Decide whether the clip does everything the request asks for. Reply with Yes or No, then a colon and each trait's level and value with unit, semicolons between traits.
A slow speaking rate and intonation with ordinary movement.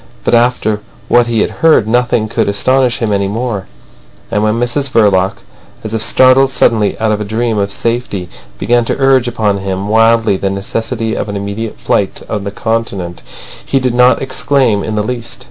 No: average, 185 wpm; average, 3.0 semitones